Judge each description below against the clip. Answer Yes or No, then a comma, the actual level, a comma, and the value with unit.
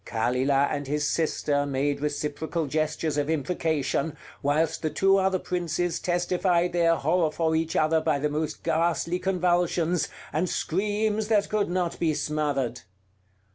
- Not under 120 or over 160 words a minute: Yes, average, 140 wpm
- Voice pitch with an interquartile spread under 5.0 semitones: Yes, average, 3.2 semitones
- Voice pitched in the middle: Yes, medium, 160 Hz